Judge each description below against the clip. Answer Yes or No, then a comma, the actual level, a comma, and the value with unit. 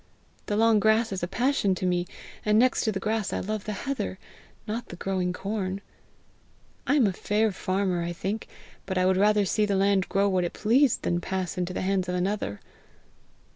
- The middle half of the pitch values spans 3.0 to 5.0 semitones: No, narrow, 2.6 semitones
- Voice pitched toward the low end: No, high, 195 Hz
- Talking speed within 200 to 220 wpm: Yes, fast, 205 wpm